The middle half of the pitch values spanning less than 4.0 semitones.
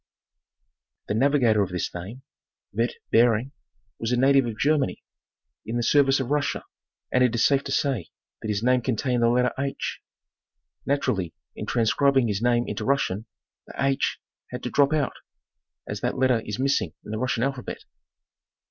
Yes: average, 3.5 semitones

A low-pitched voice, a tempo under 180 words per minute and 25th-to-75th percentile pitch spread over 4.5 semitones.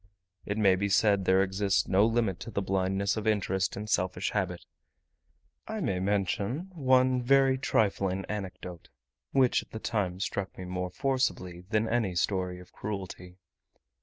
No: low, 100 Hz; average, 155 wpm; average, 3.2 semitones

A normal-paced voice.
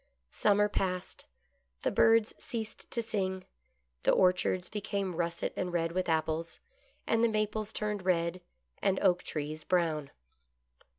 No: slow, 130 wpm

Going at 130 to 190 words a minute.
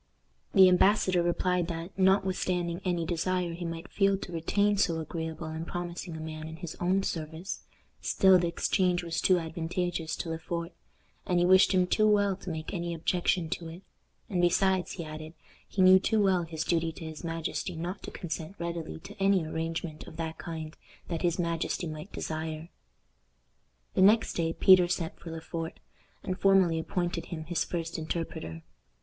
Yes: average, 180 wpm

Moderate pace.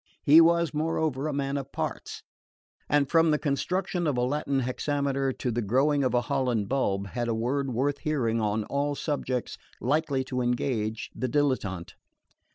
Yes: average, 165 wpm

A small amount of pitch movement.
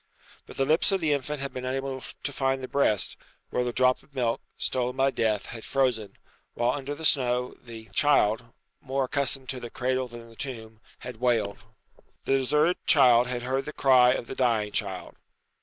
Yes: narrow, 2.3 semitones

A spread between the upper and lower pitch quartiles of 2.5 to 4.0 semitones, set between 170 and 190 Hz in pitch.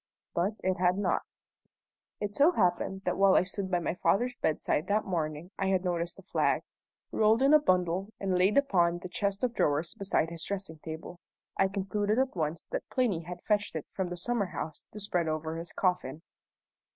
Yes: average, 3.1 semitones; medium, 185 Hz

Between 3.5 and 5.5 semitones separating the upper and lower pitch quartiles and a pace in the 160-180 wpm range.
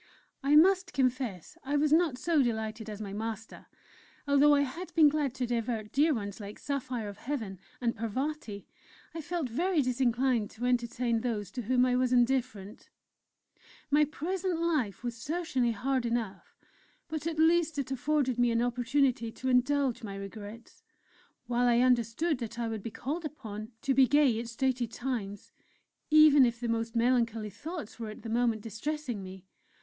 Yes: average, 4.3 semitones; average, 170 wpm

